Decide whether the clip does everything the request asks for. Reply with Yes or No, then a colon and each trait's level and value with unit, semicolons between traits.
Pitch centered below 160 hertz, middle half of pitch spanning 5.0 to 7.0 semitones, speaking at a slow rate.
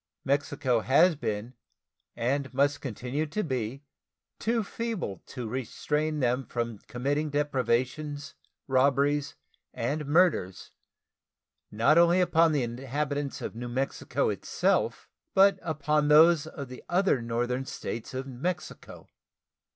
No: medium, 140 Hz; average, 3.7 semitones; slow, 115 wpm